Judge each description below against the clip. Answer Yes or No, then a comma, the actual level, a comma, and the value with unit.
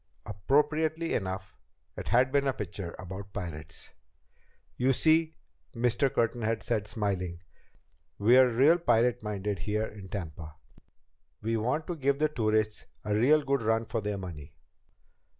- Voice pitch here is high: No, low, 110 Hz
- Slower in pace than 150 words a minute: Yes, average, 140 wpm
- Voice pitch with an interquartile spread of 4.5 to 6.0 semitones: Yes, average, 5.1 semitones